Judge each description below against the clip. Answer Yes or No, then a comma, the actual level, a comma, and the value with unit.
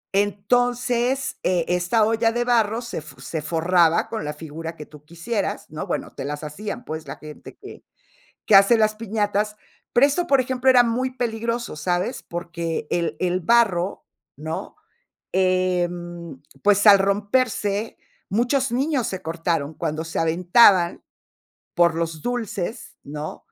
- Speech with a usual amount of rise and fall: No, wide, 5.8 semitones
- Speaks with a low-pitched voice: No, high, 195 Hz